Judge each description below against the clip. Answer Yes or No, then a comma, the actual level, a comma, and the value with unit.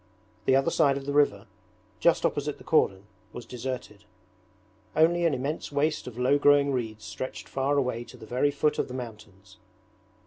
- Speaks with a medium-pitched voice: No, low, 130 Hz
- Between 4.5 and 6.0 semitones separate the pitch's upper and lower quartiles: No, average, 3.7 semitones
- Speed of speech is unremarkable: Yes, average, 175 wpm